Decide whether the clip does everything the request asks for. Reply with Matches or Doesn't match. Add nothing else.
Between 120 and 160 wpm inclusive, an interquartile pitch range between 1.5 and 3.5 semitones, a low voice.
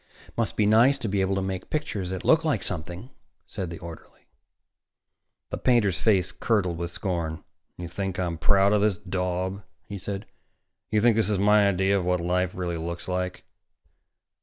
Doesn't match